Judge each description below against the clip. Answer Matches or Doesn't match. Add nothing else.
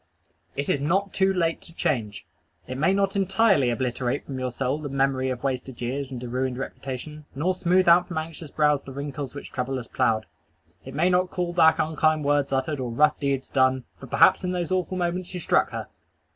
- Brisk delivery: Matches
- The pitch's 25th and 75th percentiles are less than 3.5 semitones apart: Doesn't match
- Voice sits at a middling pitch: Matches